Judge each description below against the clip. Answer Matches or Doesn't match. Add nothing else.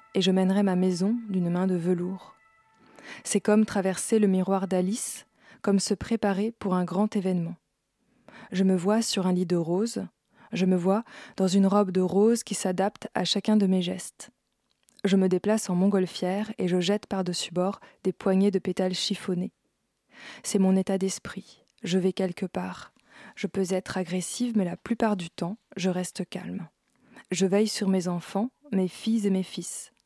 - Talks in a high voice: Matches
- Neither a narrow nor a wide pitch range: Doesn't match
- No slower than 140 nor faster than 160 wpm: Doesn't match